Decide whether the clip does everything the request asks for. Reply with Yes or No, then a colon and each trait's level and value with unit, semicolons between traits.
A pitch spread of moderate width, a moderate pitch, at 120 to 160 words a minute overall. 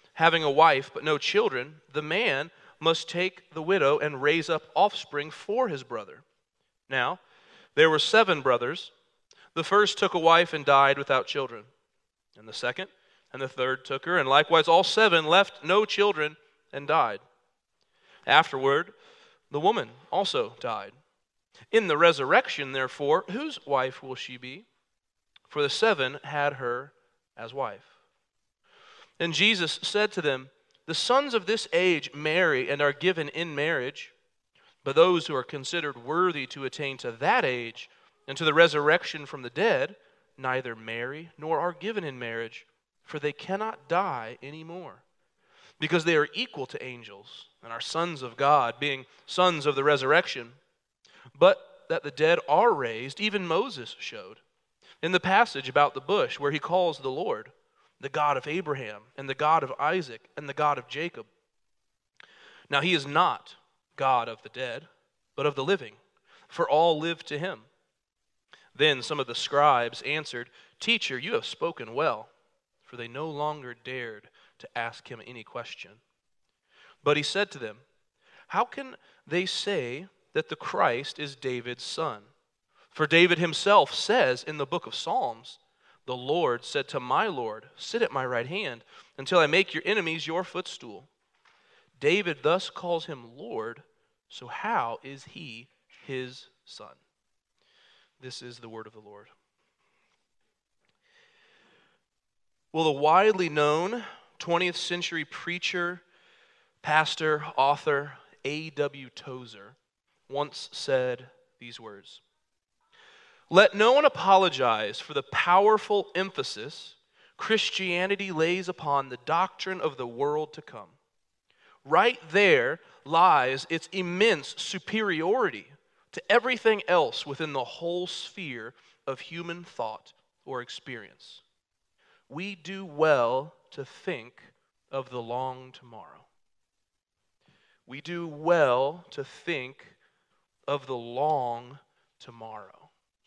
No: wide, 5.7 semitones; medium, 155 Hz; average, 140 wpm